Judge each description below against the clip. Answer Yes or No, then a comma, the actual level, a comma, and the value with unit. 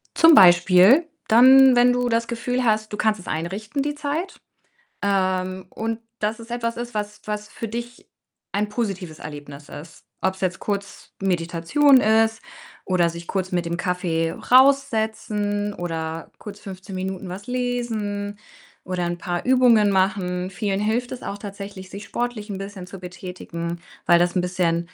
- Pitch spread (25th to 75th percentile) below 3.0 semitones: No, average, 4.2 semitones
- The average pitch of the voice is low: No, high, 200 Hz